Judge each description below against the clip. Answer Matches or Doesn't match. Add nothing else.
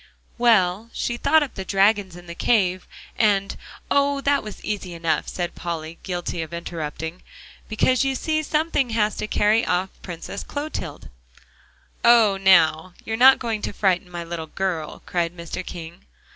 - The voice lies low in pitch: Doesn't match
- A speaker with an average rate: Matches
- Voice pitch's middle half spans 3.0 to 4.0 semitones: Doesn't match